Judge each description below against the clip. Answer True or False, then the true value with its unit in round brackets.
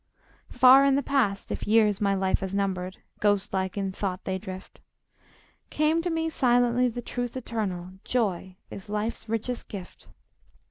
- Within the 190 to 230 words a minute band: False (155 wpm)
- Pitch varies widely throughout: False (4.3 semitones)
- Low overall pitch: False (210 Hz)